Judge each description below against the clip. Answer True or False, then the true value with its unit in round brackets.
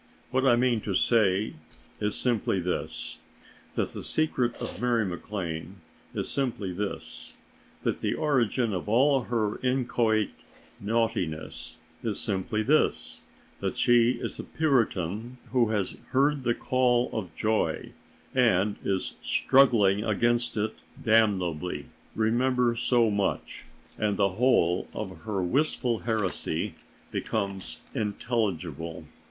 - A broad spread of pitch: False (3.9 semitones)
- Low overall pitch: True (110 Hz)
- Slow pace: True (120 wpm)